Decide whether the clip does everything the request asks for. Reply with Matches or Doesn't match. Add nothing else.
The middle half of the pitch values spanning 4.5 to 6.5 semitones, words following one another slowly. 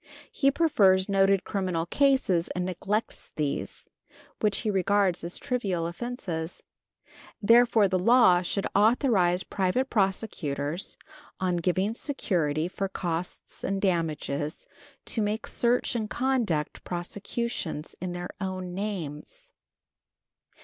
Doesn't match